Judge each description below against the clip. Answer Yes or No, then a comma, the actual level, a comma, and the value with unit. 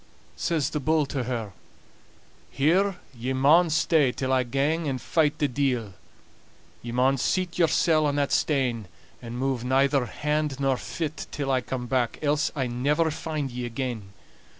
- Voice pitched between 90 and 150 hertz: Yes, low, 135 Hz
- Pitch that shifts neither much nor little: Yes, average, 3.4 semitones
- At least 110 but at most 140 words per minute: No, average, 160 wpm